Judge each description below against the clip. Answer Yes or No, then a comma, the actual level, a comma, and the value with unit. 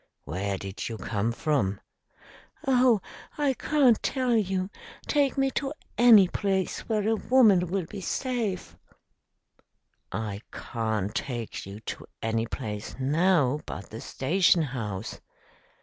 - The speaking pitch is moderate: Yes, medium, 175 Hz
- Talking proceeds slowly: Yes, slow, 125 wpm